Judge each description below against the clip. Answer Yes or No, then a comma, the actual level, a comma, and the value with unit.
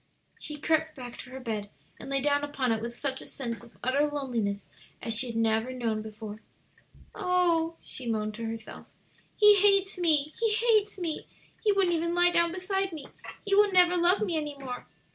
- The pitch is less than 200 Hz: No, very high, 290 Hz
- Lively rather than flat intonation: Yes, wide, 7.3 semitones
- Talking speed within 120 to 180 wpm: No, average, 195 wpm